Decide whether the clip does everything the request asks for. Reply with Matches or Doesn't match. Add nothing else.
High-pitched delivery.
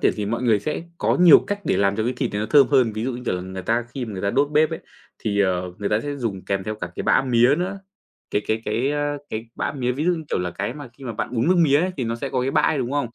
Doesn't match